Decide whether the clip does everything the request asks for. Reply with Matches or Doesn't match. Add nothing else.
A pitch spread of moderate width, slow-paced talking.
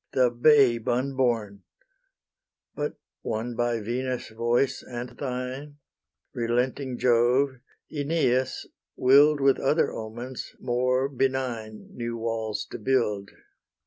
Doesn't match